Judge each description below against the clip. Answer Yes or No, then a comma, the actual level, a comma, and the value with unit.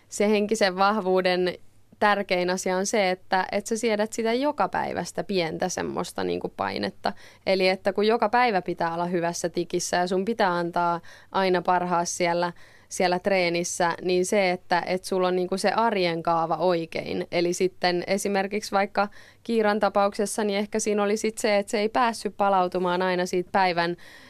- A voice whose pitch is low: No, medium, 185 Hz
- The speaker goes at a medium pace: No, fast, 170 wpm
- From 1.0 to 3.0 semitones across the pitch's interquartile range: Yes, narrow, 2.6 semitones